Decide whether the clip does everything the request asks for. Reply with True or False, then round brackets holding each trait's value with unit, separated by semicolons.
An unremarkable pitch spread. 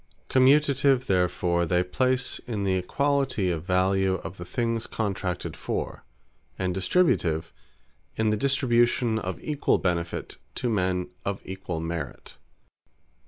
False (5.7 semitones)